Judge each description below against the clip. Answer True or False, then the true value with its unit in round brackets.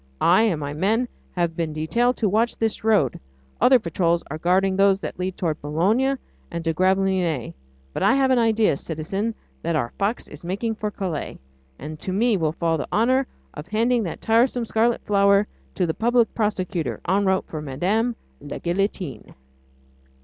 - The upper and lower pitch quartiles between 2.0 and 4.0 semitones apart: False (5.3 semitones)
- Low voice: False (195 Hz)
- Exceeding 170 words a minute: True (180 wpm)